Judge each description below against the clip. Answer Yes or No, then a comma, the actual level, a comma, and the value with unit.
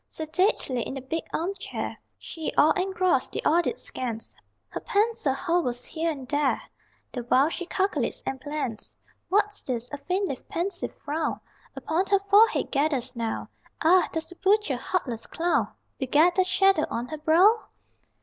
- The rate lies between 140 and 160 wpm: Yes, average, 150 wpm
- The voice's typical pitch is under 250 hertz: No, very high, 320 Hz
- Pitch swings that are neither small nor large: No, wide, 5.9 semitones